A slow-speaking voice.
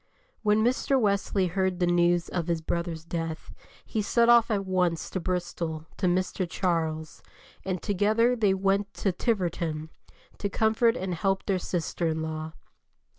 No: average, 155 wpm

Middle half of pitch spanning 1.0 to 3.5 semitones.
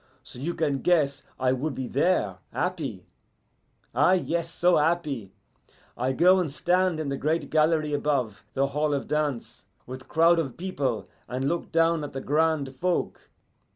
No: average, 4.0 semitones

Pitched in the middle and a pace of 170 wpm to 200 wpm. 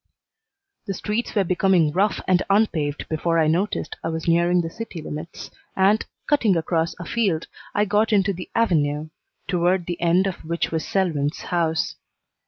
No: medium, 175 Hz; average, 160 wpm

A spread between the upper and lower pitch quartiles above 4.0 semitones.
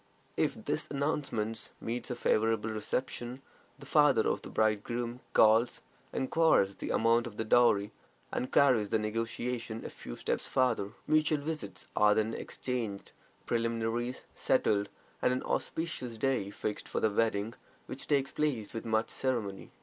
No: average, 3.0 semitones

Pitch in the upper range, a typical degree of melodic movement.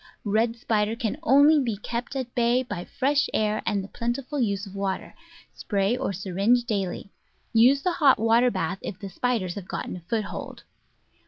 Yes: high, 225 Hz; average, 3.9 semitones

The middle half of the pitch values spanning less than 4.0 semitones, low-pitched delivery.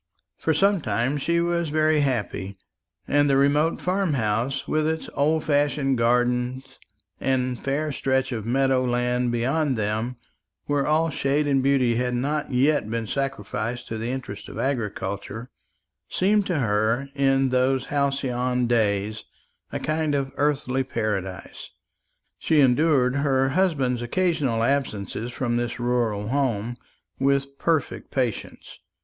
Yes: average, 3.4 semitones; low, 130 Hz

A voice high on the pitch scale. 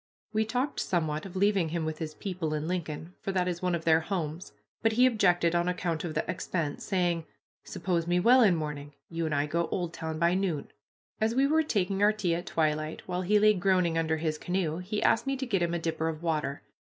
No: medium, 175 Hz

